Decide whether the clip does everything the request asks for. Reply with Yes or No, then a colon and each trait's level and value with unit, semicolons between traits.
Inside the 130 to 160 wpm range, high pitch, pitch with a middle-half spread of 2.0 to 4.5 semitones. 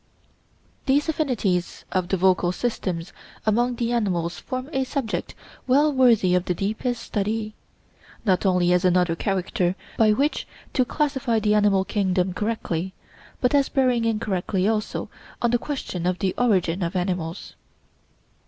No: average, 145 wpm; high, 210 Hz; average, 5.0 semitones